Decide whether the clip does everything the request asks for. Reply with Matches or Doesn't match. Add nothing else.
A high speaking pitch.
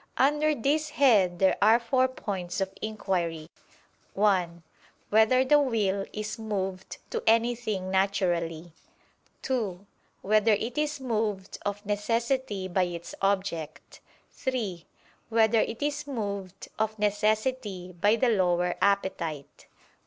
Matches